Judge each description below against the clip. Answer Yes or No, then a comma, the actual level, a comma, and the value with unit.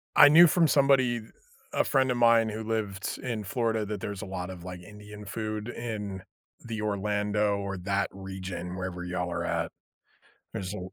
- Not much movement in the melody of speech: No, average, 3.0 semitones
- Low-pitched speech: Yes, low, 105 Hz